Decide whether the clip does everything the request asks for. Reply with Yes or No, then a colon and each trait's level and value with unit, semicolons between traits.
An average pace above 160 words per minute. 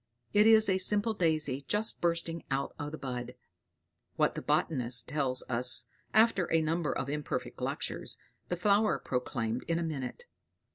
No: average, 155 wpm